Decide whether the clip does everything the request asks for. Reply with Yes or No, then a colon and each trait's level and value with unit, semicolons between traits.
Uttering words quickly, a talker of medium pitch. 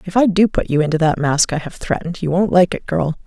Yes: fast, 295 wpm; medium, 170 Hz